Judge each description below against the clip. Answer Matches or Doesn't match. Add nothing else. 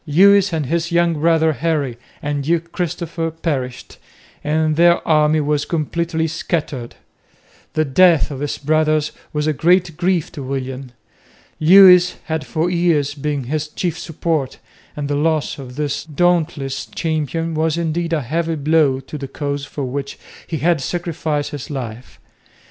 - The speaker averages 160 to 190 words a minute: Doesn't match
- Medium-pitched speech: Matches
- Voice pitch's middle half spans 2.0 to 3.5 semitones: Matches